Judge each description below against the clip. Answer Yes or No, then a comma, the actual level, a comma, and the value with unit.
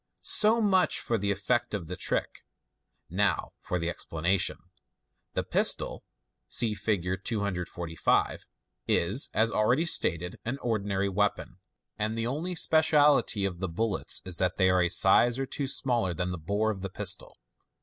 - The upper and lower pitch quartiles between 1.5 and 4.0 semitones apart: No, average, 4.7 semitones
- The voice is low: Yes, low, 100 Hz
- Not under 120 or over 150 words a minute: No, average, 160 wpm